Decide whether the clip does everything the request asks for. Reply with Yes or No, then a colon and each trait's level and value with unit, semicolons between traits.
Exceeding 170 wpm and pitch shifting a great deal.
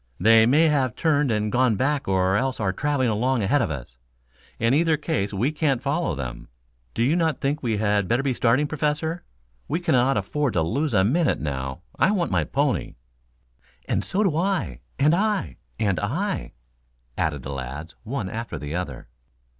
Yes: average, 180 wpm; wide, 7.8 semitones